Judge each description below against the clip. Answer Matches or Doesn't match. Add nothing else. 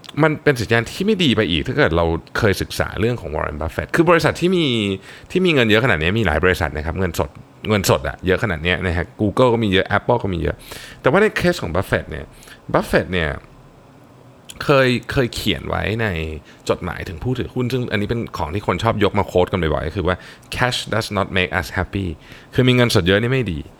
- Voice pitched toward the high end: Doesn't match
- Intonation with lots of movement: Matches